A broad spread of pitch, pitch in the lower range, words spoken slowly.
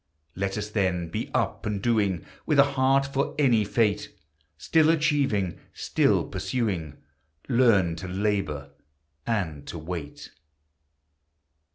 Yes: wide, 6.6 semitones; low, 105 Hz; slow, 115 wpm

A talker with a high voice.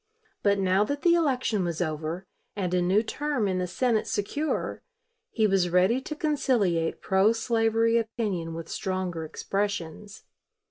Yes: high, 200 Hz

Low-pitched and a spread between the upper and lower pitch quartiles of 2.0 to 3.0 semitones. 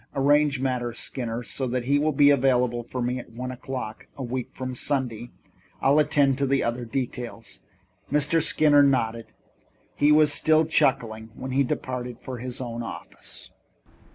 Yes: low, 130 Hz; average, 2.7 semitones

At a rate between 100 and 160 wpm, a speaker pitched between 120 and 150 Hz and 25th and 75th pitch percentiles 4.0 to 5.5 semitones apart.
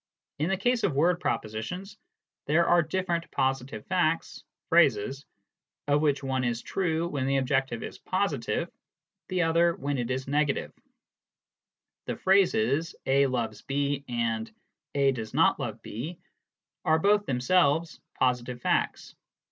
Yes: average, 145 wpm; medium, 140 Hz; average, 5.0 semitones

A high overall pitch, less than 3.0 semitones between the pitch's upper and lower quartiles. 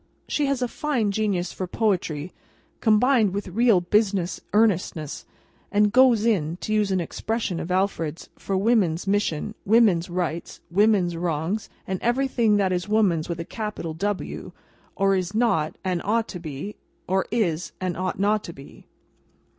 No: high, 195 Hz; average, 3.8 semitones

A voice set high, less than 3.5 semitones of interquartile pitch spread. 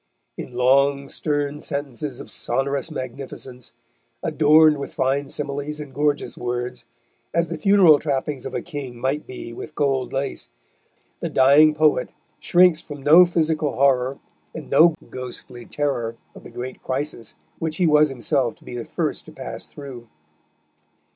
No: medium, 140 Hz; average, 2.7 semitones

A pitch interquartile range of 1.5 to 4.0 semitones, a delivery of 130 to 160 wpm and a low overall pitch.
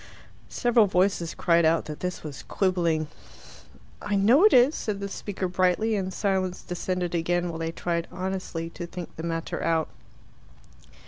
No: average, 2.8 semitones; average, 155 wpm; medium, 180 Hz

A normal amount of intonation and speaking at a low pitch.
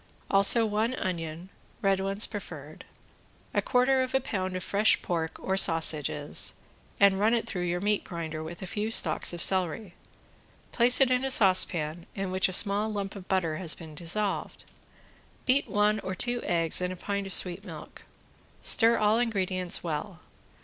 No: average, 3.6 semitones; high, 190 Hz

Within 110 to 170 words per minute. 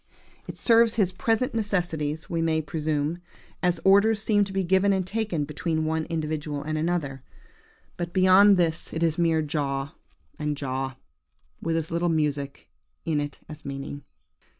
Yes: average, 155 wpm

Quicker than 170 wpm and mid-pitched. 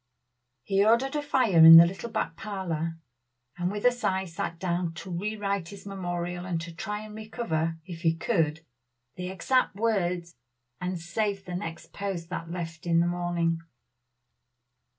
No: average, 160 wpm; medium, 180 Hz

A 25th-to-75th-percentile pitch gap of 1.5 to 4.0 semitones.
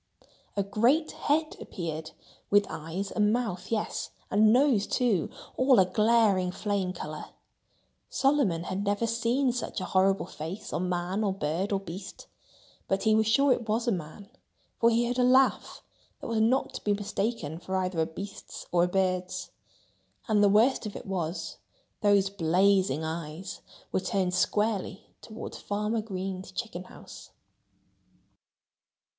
Yes: average, 3.6 semitones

